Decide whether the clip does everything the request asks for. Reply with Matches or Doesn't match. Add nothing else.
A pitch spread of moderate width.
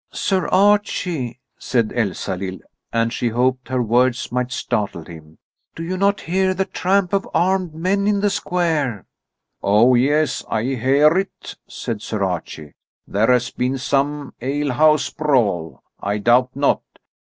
Doesn't match